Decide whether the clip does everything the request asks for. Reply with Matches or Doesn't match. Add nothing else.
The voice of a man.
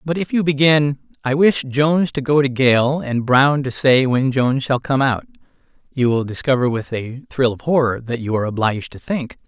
Matches